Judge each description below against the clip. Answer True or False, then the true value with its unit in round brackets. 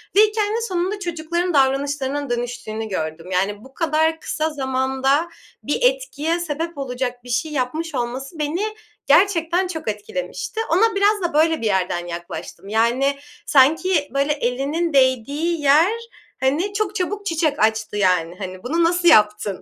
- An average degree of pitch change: False (5.8 semitones)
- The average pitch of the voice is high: True (290 Hz)